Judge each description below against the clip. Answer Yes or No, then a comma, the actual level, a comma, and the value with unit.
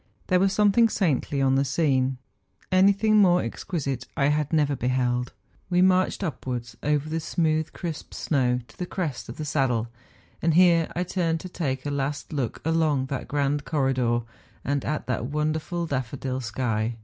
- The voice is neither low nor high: Yes, medium, 145 Hz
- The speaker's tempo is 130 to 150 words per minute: No, average, 170 wpm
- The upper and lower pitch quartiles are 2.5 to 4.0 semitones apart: No, average, 4.4 semitones